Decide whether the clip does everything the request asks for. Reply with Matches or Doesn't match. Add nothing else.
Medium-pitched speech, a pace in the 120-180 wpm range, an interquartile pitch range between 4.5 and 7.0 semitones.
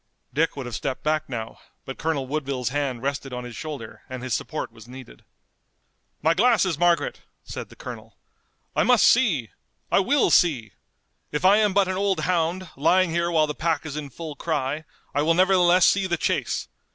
Doesn't match